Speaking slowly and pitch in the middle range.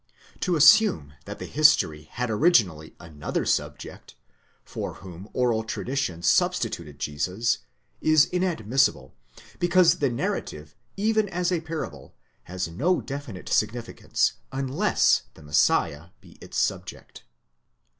No: slow, 115 wpm; low, 120 Hz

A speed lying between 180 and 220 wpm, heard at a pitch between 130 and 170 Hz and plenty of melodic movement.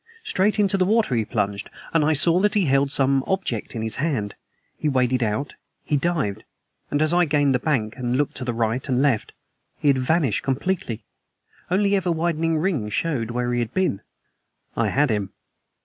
Yes: average, 190 wpm; medium, 140 Hz; wide, 5.7 semitones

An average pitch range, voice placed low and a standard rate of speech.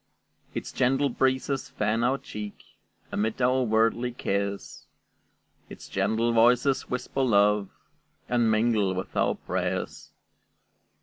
No: average, 3.2 semitones; low, 115 Hz; slow, 110 wpm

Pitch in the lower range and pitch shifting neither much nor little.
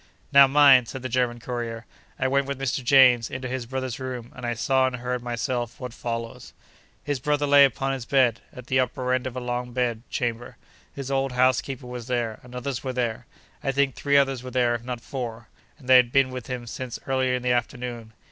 No: low, 125 Hz; narrow, 1.7 semitones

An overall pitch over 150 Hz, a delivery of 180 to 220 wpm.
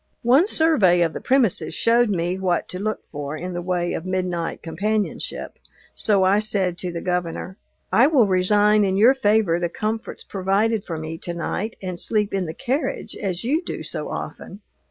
Yes: high, 190 Hz; average, 185 wpm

